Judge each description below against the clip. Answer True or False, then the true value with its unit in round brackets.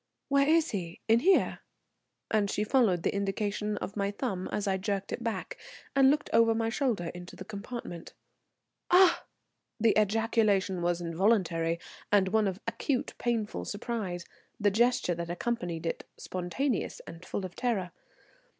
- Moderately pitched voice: False (205 Hz)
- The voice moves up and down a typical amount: True (4.2 semitones)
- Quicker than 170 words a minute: False (150 wpm)